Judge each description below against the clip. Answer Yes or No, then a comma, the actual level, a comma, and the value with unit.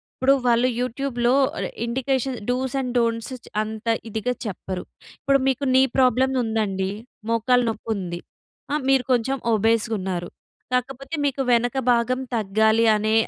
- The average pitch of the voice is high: Yes, high, 240 Hz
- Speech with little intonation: No, average, 3.1 semitones